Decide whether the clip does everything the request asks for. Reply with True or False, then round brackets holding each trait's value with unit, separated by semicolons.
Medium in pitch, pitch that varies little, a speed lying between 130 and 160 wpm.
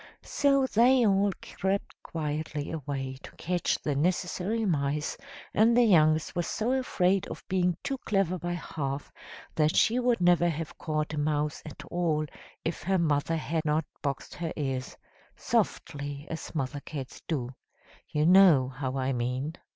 False (160 Hz; 4.4 semitones; 155 wpm)